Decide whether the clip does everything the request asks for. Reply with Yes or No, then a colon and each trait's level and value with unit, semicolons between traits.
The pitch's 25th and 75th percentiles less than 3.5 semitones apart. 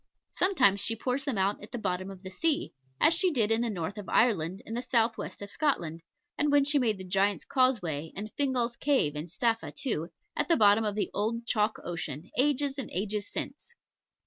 No: average, 5.2 semitones